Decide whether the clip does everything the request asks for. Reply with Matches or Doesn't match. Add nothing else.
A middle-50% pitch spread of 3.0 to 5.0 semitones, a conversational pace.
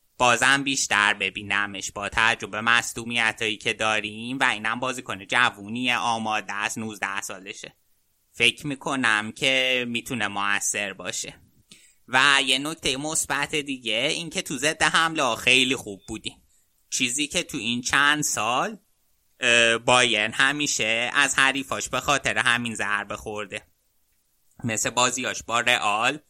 Matches